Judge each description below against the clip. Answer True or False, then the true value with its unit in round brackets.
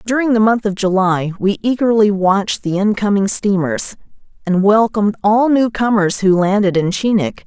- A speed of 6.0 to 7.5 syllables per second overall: False (4.9 syllables/s)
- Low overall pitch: False (205 Hz)